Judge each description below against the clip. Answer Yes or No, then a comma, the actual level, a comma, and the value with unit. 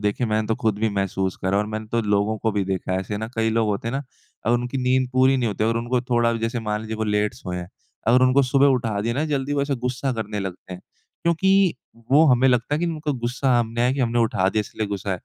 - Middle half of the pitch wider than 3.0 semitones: Yes, average, 3.6 semitones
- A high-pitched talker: No, low, 115 Hz